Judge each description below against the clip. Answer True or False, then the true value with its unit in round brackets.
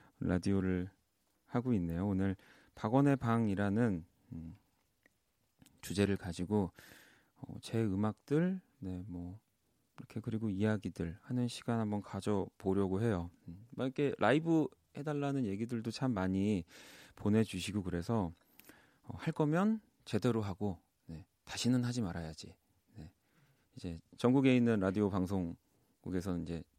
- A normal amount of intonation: True (4.8 semitones)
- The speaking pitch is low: True (105 Hz)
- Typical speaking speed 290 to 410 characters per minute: False (265 characters per minute)